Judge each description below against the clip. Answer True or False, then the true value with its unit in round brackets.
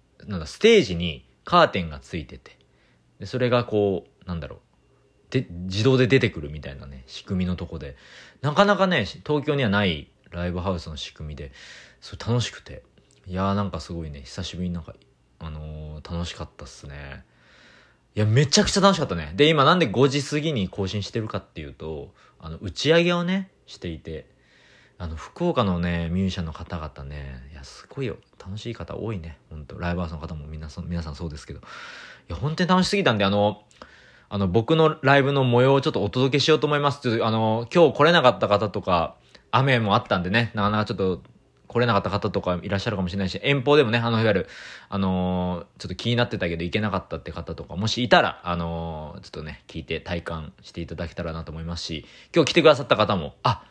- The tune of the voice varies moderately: False (6.5 semitones)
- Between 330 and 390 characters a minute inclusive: False (420 characters per minute)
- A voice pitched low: True (100 Hz)